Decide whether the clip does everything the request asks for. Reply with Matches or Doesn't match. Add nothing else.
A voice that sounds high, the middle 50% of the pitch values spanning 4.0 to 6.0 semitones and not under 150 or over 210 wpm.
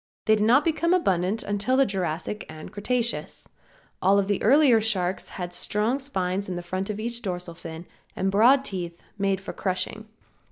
Matches